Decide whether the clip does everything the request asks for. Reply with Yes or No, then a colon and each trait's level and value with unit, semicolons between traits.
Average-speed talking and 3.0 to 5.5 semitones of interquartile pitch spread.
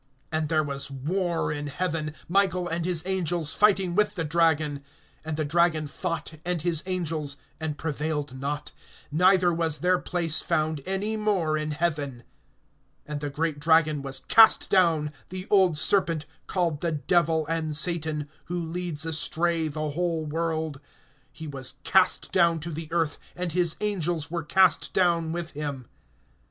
No: average, 155 wpm; narrow, 2.6 semitones